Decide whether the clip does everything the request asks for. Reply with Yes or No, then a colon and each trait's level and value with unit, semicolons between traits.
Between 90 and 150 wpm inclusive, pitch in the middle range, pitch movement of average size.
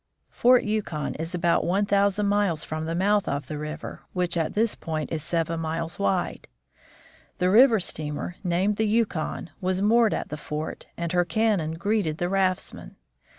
No: average, 170 wpm; medium, 180 Hz; average, 4.3 semitones